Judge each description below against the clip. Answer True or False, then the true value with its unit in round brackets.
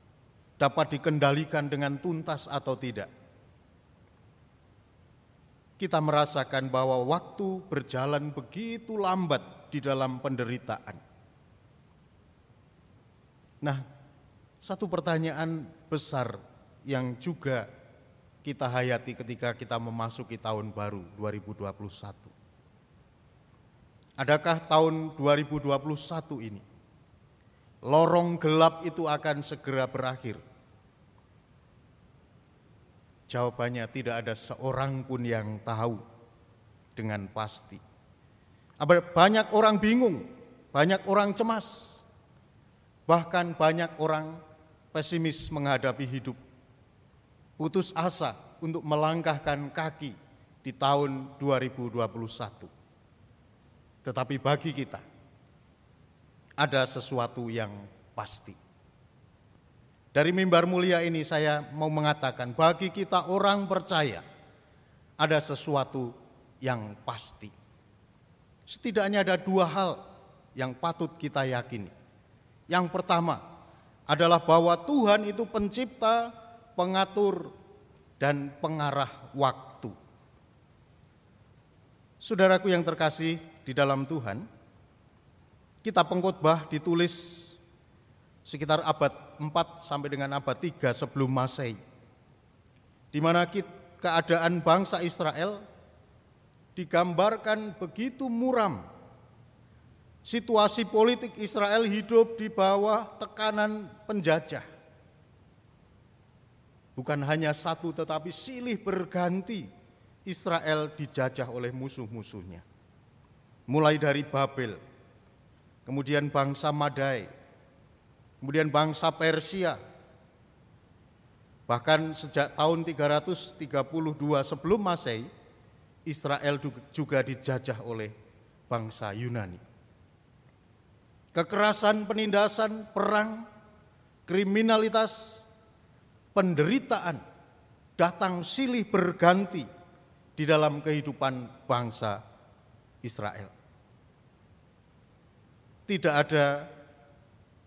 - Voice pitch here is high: False (145 Hz)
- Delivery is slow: True (75 wpm)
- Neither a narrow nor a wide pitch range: False (5.7 semitones)